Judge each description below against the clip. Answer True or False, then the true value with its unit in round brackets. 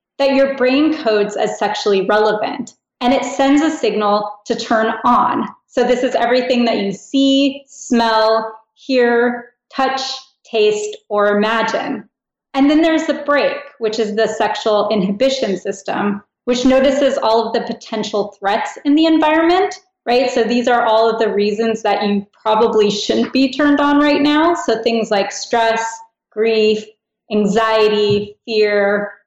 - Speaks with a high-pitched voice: True (230 Hz)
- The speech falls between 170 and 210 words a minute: False (150 wpm)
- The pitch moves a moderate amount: True (4.3 semitones)